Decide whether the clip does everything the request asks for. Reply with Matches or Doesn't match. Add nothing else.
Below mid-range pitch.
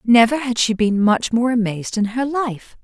Doesn't match